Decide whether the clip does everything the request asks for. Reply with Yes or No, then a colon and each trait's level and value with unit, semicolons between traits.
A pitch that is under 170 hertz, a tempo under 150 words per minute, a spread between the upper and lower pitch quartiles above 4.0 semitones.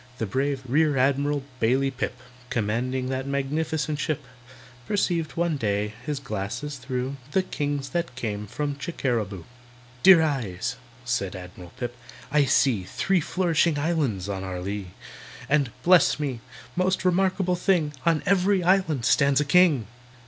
Yes: medium, 140 Hz; average, 140 wpm; average, 5.2 semitones